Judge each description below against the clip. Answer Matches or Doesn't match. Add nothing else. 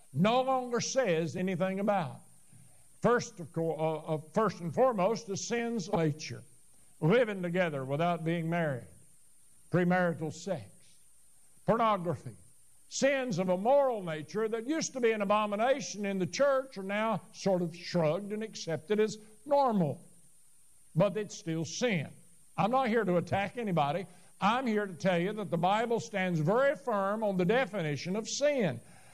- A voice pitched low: Doesn't match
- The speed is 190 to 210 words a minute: Doesn't match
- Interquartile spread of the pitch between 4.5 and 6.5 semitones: Matches